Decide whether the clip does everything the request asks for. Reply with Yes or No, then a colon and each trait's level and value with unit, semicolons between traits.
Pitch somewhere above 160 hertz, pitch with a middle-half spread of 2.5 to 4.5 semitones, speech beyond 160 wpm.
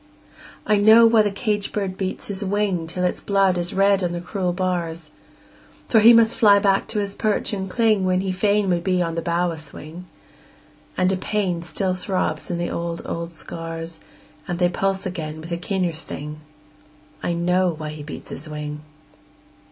Yes: medium, 185 Hz; average, 2.9 semitones; average, 190 wpm